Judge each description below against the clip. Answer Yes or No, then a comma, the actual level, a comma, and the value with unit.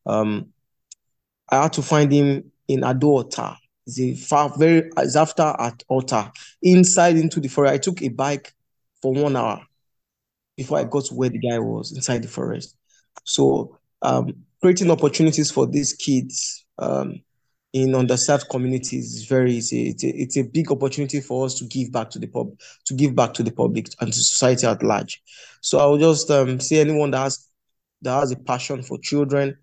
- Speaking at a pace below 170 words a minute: No, average, 185 wpm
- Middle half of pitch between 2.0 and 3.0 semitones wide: Yes, narrow, 2.6 semitones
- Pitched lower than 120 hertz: No, low, 135 Hz